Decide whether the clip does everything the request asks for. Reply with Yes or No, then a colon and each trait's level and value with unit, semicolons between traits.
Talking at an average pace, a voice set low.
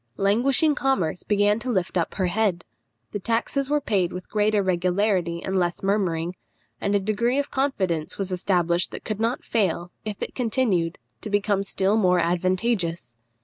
No: average, 165 wpm; high, 195 Hz